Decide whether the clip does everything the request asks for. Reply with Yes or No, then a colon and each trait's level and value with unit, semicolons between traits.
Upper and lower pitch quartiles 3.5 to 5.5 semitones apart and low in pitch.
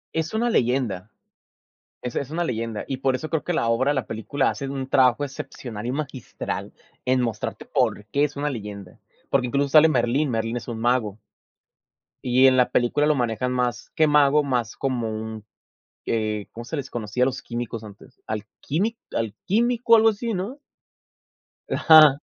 Yes: average, 4.3 semitones; low, 130 Hz